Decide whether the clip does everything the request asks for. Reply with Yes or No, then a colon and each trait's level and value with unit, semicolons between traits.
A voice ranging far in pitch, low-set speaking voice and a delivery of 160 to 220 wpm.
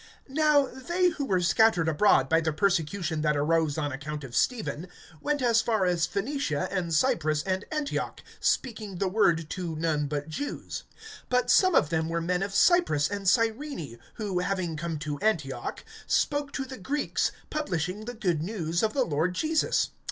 No: wide, 7.2 semitones; medium, 185 Hz; average, 175 wpm